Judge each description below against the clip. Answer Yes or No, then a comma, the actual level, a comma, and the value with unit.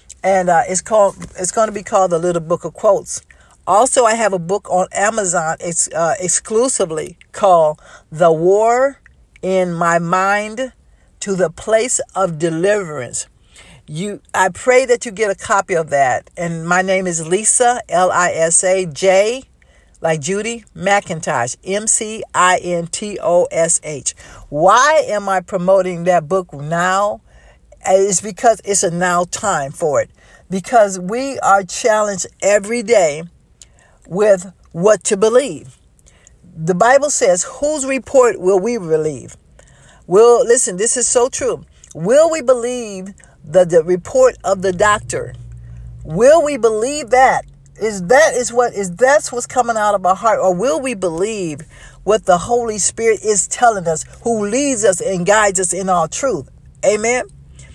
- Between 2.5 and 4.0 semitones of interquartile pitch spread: No, average, 4.8 semitones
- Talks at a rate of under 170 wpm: Yes, average, 160 wpm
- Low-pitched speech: No, high, 195 Hz